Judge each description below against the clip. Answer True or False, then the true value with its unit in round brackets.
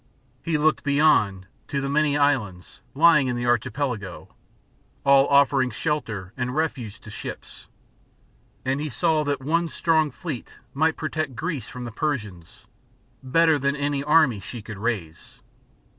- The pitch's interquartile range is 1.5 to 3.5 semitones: False (4.5 semitones)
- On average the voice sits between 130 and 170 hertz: True (140 Hz)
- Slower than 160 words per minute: True (145 wpm)